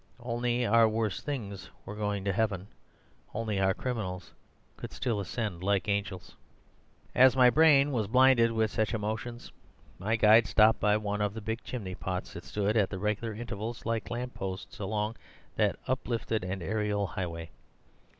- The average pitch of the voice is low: Yes, low, 110 Hz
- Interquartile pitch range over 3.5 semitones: No, average, 2.7 semitones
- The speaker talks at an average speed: Yes, average, 160 wpm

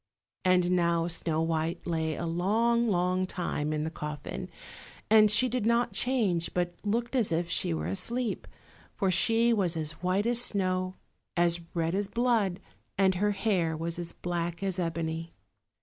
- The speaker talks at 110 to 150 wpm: No, average, 165 wpm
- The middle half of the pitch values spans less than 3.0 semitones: No, average, 3.9 semitones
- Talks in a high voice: No, medium, 180 Hz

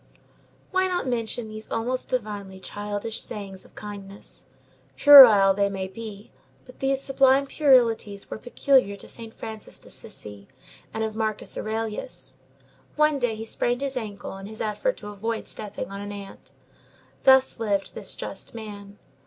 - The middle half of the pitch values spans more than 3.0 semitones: Yes, average, 3.7 semitones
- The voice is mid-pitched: No, high, 220 Hz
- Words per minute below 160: Yes, average, 150 wpm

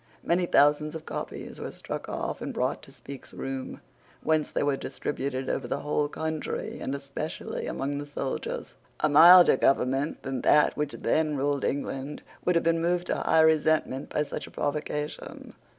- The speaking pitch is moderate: Yes, medium, 145 Hz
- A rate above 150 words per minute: Yes, average, 170 wpm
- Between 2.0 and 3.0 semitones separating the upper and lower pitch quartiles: Yes, narrow, 2.4 semitones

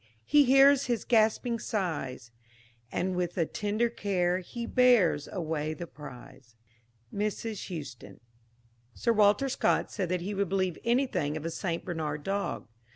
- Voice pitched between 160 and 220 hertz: Yes, high, 190 Hz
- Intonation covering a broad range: Yes, wide, 6.0 semitones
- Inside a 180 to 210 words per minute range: No, average, 145 wpm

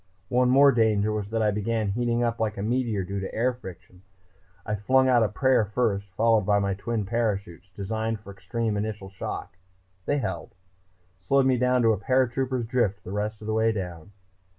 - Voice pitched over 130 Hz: No, low, 110 Hz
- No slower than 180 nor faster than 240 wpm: Yes, average, 190 wpm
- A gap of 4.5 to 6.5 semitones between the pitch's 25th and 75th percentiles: No, average, 3.2 semitones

